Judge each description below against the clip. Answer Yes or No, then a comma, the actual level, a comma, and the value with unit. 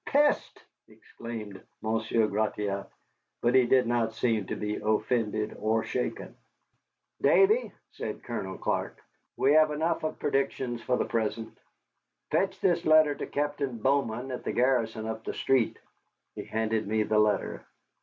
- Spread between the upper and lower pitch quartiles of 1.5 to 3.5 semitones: No, average, 4.0 semitones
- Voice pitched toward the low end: Yes, low, 115 Hz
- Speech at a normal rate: Yes, average, 145 wpm